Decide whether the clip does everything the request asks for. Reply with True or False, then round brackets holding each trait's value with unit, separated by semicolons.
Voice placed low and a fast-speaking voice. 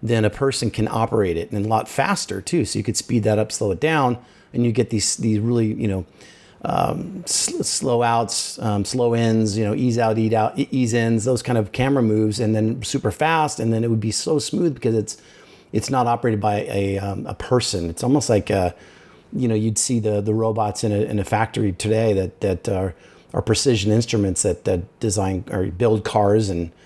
True (110 Hz; 220 wpm)